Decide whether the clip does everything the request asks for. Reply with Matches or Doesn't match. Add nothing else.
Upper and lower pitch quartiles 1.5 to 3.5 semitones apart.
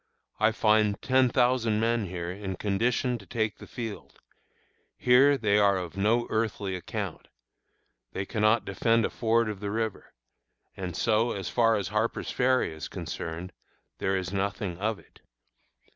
Matches